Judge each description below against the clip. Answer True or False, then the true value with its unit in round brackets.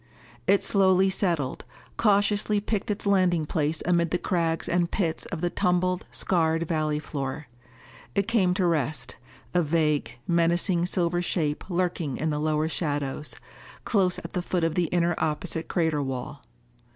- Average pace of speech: True (150 wpm)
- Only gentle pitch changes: False (3.0 semitones)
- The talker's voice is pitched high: False (170 Hz)